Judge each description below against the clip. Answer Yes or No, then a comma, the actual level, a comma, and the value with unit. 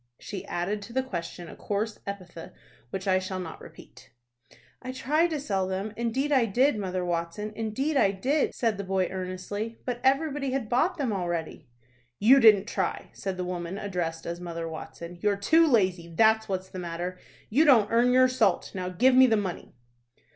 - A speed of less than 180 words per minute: No, average, 185 wpm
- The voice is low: No, high, 205 Hz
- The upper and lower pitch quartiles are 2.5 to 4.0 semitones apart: No, wide, 5.4 semitones